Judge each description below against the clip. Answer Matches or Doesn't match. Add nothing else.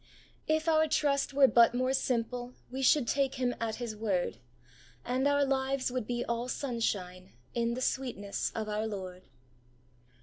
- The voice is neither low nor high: Doesn't match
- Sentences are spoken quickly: Doesn't match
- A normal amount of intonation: Matches